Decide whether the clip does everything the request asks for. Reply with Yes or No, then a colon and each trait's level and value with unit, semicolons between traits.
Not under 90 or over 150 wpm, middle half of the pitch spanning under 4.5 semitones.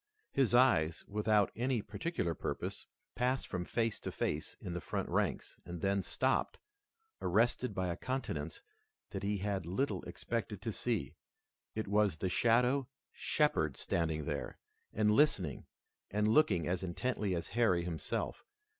No: average, 145 wpm; wide, 5.4 semitones